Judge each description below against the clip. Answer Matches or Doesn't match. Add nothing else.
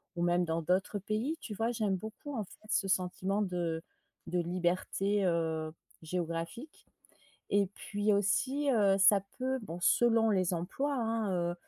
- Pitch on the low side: Doesn't match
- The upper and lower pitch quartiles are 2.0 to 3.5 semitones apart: Doesn't match